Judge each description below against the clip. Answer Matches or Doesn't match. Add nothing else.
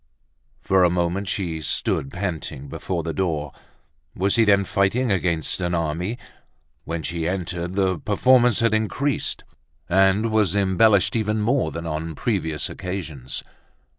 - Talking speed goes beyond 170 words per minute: Doesn't match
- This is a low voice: Matches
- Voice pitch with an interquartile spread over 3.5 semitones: Matches